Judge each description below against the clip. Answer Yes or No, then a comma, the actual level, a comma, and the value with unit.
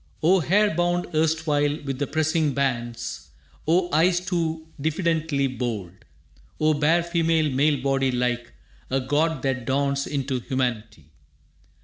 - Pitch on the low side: No, medium, 145 Hz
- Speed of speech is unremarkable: No, slow, 125 wpm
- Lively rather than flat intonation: No, average, 3.7 semitones